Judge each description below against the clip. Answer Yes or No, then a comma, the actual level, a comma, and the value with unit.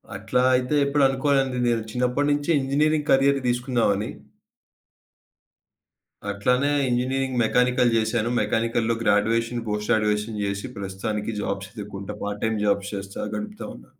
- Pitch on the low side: Yes, low, 115 Hz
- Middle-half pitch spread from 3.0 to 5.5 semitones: Yes, average, 3.8 semitones